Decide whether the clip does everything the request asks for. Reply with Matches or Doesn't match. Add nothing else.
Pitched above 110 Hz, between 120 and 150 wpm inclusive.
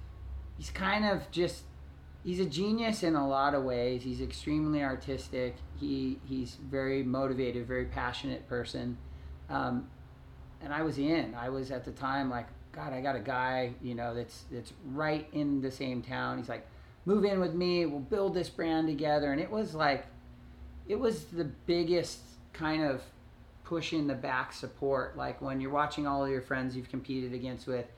Doesn't match